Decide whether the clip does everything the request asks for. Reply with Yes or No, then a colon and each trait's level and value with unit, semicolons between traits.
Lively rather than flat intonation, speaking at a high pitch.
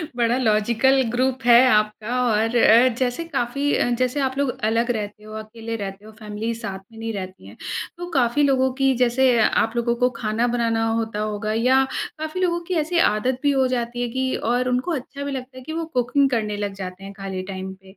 No: average, 3.4 semitones; high, 235 Hz